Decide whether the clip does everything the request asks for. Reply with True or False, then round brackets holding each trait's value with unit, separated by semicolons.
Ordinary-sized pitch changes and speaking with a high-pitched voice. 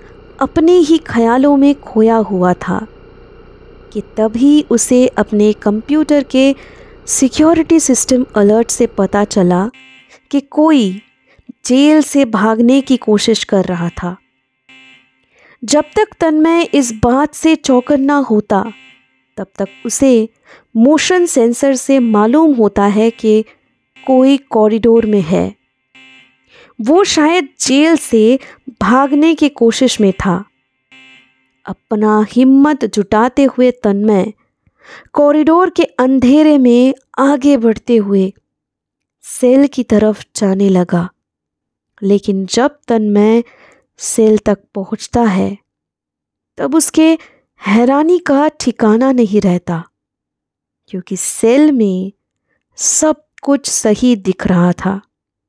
False (5.9 semitones; 230 Hz)